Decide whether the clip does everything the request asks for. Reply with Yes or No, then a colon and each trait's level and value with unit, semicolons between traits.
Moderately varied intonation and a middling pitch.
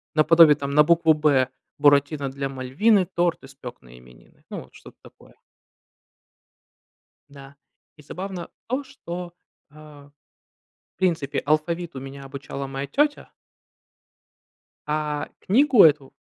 Yes: average, 3.8 semitones; medium, 150 Hz